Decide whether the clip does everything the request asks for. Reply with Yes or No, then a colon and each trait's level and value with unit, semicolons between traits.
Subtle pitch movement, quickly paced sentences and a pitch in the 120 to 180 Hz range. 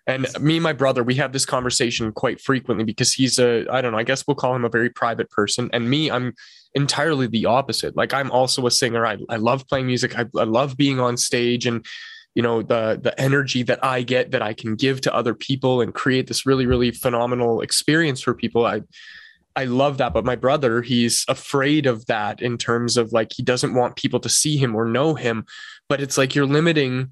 Yes: narrow, 2.3 semitones; fast, 230 wpm; low, 125 Hz